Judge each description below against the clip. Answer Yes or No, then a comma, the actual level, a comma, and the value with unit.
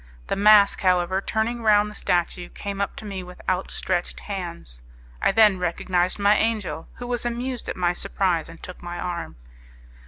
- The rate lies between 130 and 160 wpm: No, average, 175 wpm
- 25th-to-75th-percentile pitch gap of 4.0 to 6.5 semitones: No, average, 3.1 semitones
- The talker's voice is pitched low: No, high, 190 Hz